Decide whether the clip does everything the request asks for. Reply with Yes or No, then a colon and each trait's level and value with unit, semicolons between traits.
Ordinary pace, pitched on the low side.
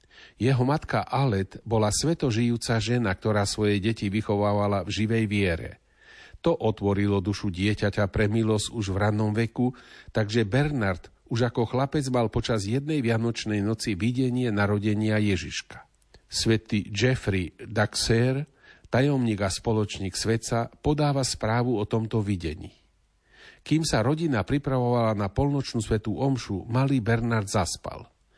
Yes: average, 125 wpm; low, 110 Hz